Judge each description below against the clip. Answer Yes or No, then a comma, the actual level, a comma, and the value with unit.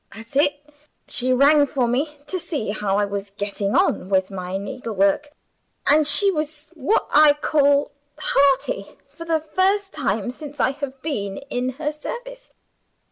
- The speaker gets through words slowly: No, average, 155 wpm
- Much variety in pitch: Yes, wide, 6.3 semitones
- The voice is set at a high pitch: Yes, very high, 280 Hz